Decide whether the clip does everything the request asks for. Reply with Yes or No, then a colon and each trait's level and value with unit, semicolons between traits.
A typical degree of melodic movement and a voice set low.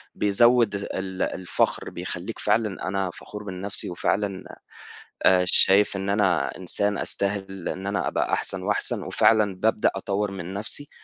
No: narrow, 1.6 semitones; low, 100 Hz